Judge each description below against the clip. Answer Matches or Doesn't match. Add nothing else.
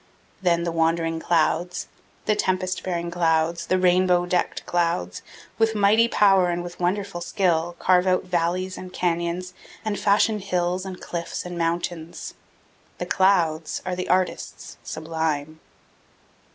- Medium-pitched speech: Matches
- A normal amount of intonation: Doesn't match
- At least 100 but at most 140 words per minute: Matches